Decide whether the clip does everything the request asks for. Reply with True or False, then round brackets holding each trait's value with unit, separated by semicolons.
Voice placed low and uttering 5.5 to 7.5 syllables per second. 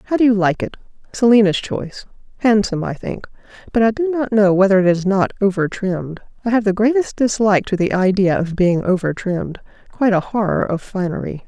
False (200 Hz; 5.9 syllables/s)